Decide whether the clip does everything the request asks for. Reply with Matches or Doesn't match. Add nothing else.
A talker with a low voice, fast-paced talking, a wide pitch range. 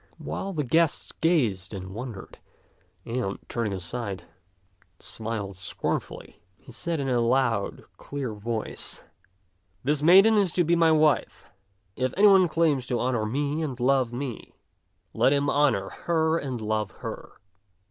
Doesn't match